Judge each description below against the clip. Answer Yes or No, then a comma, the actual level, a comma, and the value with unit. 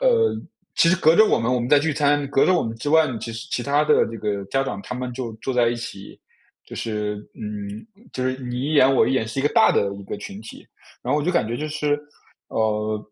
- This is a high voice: No, low, 125 Hz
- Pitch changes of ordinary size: Yes, average, 5.0 semitones